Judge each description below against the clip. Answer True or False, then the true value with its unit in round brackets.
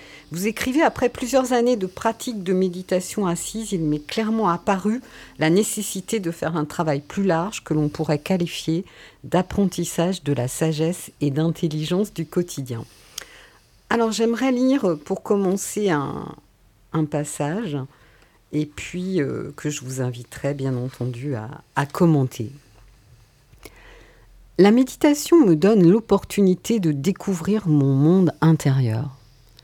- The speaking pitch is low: False (165 Hz)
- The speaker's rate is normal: False (130 wpm)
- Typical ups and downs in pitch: False (6.1 semitones)